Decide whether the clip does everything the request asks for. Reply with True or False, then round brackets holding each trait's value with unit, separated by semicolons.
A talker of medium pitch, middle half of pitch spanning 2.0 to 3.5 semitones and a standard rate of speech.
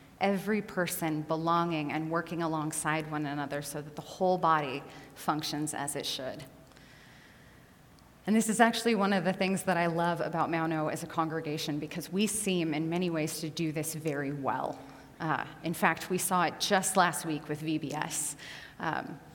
True (160 Hz; 2.9 semitones; 175 wpm)